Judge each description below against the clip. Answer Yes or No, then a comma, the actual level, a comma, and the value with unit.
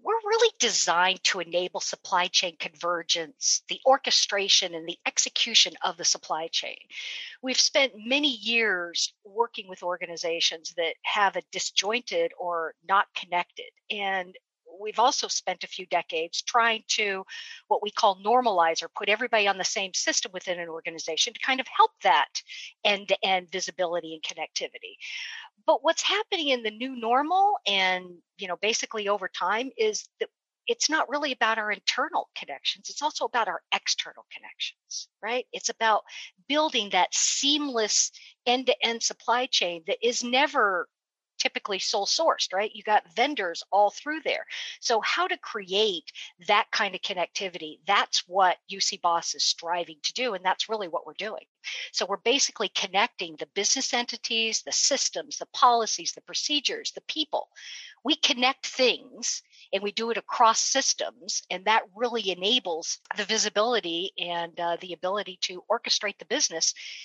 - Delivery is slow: No, average, 155 wpm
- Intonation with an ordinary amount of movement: No, wide, 6.4 semitones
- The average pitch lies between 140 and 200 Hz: No, high, 215 Hz